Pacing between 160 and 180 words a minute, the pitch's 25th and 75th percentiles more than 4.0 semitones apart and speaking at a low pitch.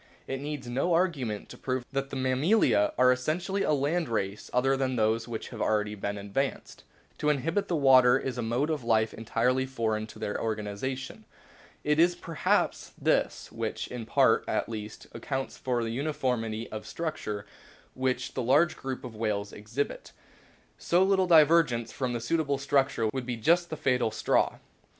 Yes: average, 175 wpm; average, 4.6 semitones; low, 130 Hz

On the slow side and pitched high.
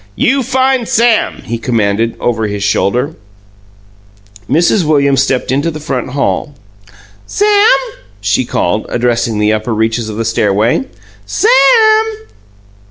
No: slow, 120 wpm; low, 125 Hz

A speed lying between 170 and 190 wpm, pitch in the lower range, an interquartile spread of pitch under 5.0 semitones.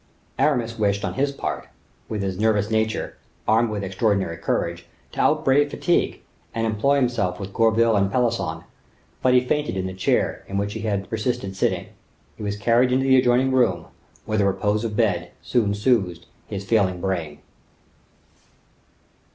No: average, 160 wpm; low, 110 Hz; average, 3.6 semitones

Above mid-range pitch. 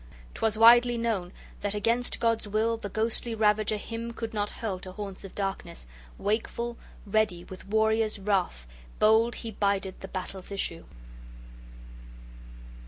Yes: high, 215 Hz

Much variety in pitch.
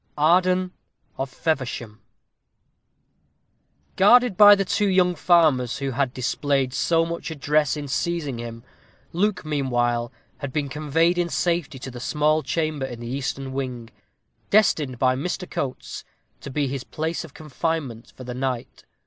No: average, 4.6 semitones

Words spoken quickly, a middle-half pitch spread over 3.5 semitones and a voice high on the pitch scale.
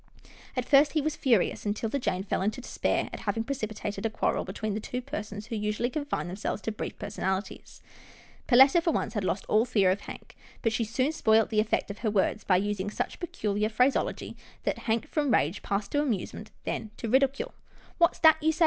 Yes: fast, 210 wpm; average, 4.7 semitones; high, 220 Hz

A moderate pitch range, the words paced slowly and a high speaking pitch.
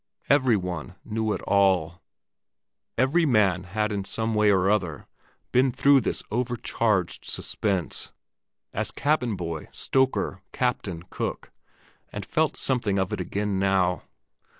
No: average, 4.5 semitones; slow, 120 wpm; low, 105 Hz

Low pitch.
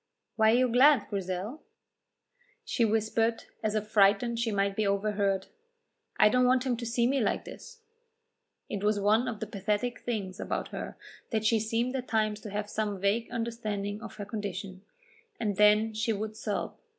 No: high, 215 Hz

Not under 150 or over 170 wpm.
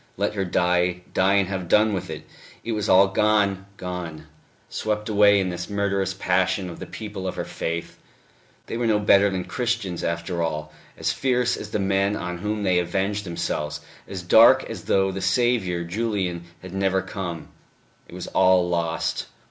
No: average, 180 wpm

